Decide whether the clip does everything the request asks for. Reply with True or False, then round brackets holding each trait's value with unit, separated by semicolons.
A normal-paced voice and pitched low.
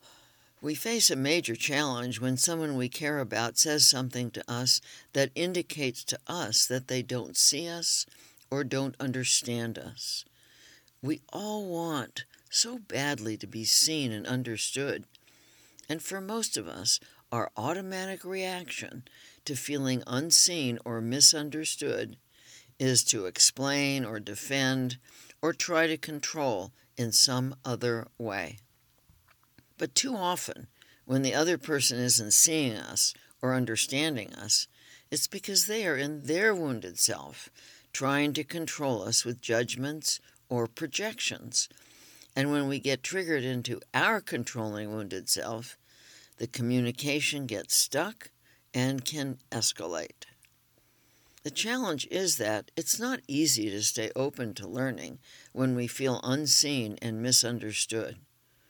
False (130 wpm; 130 Hz)